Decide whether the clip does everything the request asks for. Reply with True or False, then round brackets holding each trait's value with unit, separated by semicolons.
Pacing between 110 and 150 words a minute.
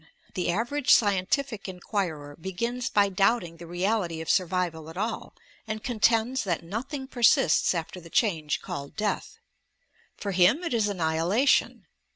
True (140 wpm)